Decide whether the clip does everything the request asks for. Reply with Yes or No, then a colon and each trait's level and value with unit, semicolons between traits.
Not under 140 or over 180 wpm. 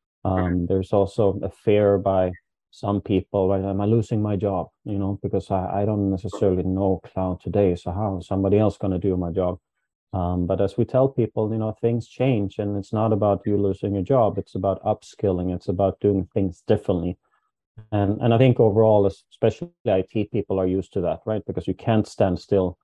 No: fast, 205 wpm